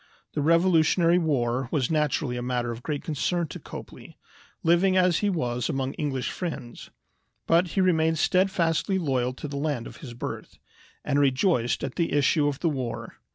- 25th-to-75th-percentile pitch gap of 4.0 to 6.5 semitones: Yes, average, 4.8 semitones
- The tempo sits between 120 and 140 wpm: No, average, 170 wpm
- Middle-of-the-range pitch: Yes, medium, 150 Hz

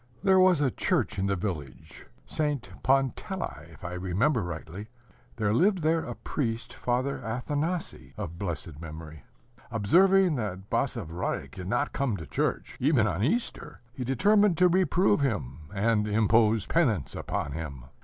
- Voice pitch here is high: No, low, 115 Hz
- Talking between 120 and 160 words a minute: Yes, average, 145 wpm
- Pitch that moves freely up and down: Yes, wide, 9.0 semitones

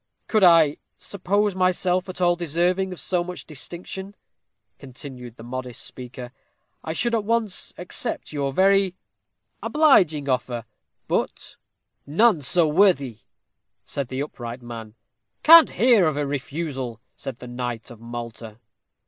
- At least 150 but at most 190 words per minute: No, slow, 135 wpm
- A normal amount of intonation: No, wide, 6.8 semitones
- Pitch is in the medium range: Yes, medium, 155 Hz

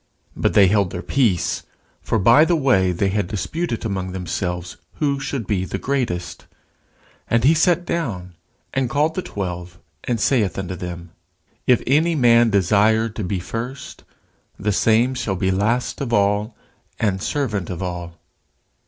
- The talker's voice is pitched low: Yes, low, 105 Hz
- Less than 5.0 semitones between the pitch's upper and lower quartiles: No, wide, 5.4 semitones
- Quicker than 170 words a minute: No, average, 155 wpm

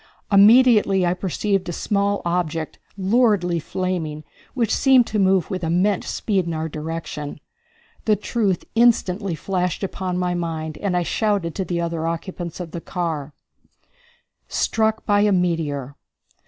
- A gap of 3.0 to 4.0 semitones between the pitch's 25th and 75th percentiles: Yes, average, 3.5 semitones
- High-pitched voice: No, medium, 180 Hz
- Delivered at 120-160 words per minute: Yes, average, 140 wpm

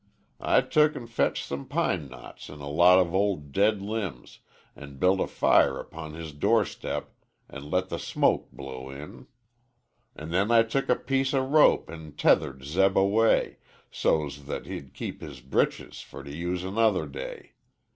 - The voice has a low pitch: Yes, very low, 85 Hz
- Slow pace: No, average, 170 wpm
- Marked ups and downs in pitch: Yes, wide, 7.1 semitones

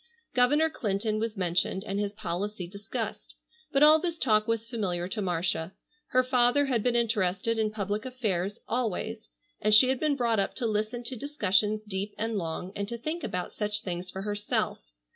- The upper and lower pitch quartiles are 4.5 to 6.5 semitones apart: No, average, 3.7 semitones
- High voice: Yes, high, 215 Hz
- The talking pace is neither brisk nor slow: Yes, average, 180 wpm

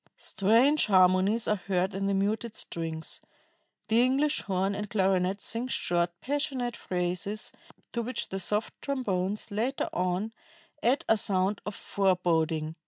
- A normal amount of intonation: Yes, average, 3.9 semitones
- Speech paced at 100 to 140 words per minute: Yes, slow, 135 wpm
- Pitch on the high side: Yes, high, 200 Hz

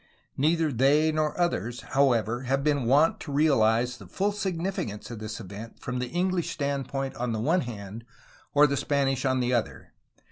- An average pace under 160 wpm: No, average, 180 wpm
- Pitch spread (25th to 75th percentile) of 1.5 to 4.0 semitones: No, average, 4.4 semitones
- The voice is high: No, low, 135 Hz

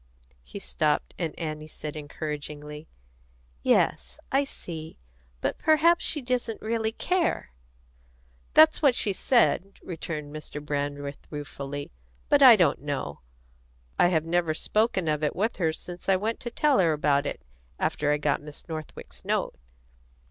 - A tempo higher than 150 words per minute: No, average, 145 wpm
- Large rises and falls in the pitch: Yes, wide, 6.8 semitones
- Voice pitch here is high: No, medium, 160 Hz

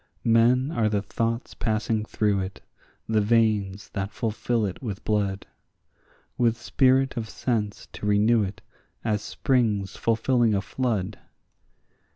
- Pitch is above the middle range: No, low, 110 Hz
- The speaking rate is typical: No, slow, 130 wpm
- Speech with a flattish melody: Yes, narrow, 2.3 semitones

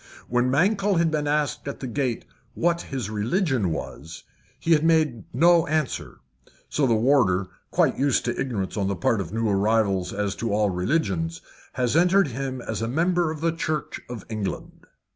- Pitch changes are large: Yes, wide, 6.9 semitones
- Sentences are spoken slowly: No, average, 180 wpm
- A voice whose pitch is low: Yes, low, 130 Hz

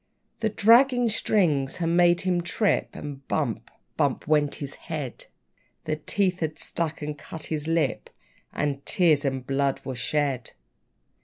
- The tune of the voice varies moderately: Yes, average, 3.9 semitones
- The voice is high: No, medium, 155 Hz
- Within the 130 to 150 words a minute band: Yes, average, 145 wpm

